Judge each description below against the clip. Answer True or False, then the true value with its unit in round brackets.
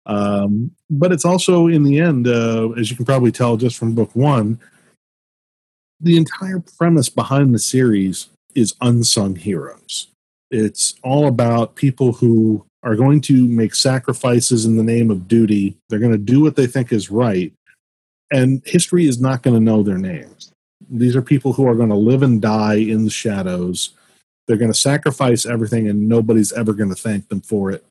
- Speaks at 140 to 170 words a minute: False (185 wpm)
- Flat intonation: False (3.7 semitones)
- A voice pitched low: True (120 Hz)